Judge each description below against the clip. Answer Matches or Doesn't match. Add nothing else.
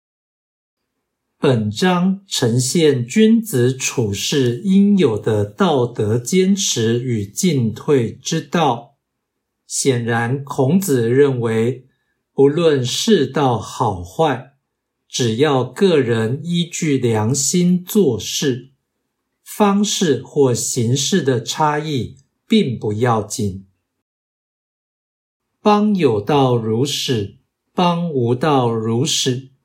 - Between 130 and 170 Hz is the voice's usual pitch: Matches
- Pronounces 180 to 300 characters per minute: Doesn't match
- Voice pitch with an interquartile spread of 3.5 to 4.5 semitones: Doesn't match